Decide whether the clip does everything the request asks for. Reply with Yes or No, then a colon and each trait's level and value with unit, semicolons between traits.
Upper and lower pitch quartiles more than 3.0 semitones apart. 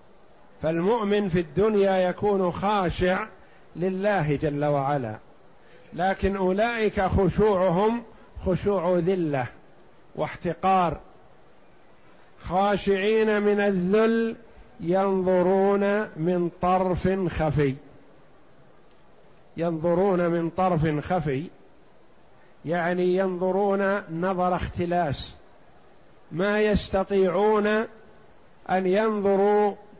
No: average, 2.7 semitones